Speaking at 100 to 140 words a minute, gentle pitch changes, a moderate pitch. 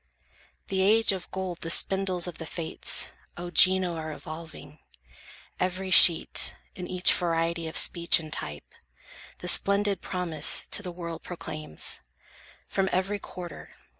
Yes: slow, 135 wpm; narrow, 2.3 semitones; medium, 180 Hz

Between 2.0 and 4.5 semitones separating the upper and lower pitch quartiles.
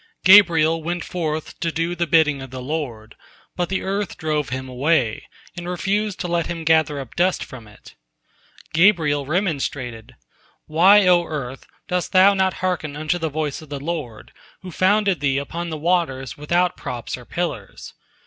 Yes: average, 4.0 semitones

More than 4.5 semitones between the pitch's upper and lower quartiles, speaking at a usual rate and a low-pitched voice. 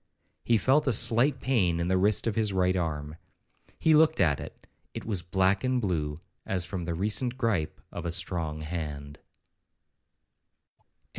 Yes: wide, 5.5 semitones; average, 160 wpm; very low, 95 Hz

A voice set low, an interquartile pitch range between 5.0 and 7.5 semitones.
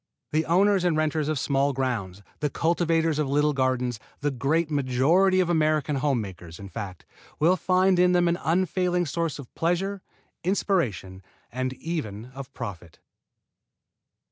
No: medium, 150 Hz; average, 5.3 semitones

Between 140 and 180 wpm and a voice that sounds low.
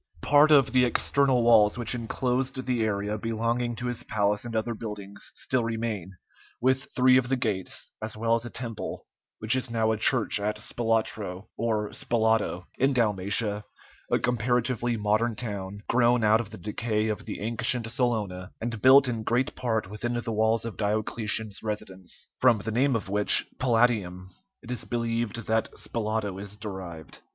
Yes: average, 170 wpm; low, 115 Hz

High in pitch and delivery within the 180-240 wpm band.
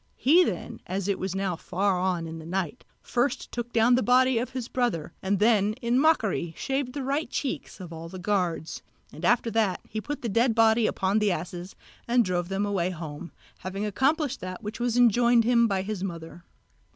Yes: high, 210 Hz; average, 200 wpm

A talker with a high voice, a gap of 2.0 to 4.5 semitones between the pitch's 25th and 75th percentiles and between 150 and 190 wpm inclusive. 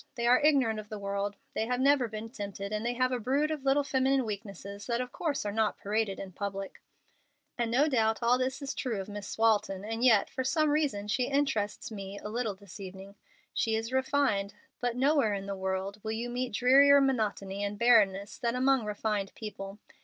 No: high, 225 Hz; average, 4.2 semitones; fast, 205 wpm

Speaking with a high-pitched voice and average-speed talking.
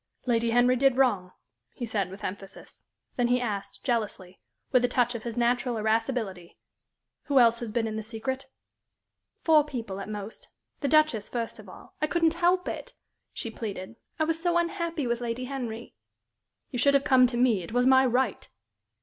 Yes: high, 245 Hz; average, 185 wpm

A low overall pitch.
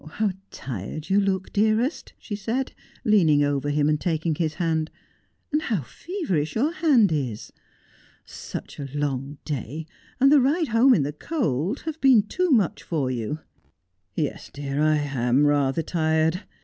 No: medium, 160 Hz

